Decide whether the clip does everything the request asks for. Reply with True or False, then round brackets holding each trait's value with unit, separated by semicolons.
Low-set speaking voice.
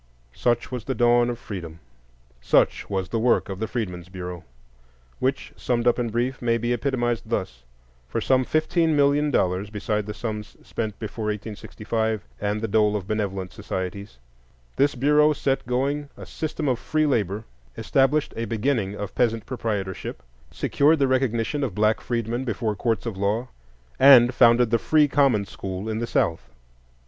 True (115 Hz)